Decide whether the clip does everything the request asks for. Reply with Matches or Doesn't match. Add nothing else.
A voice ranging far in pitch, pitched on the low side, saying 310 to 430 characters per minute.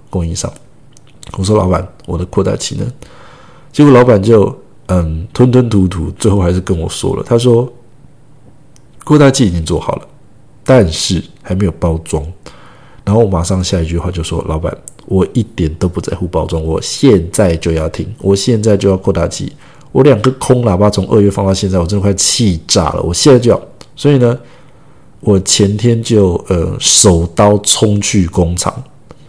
Doesn't match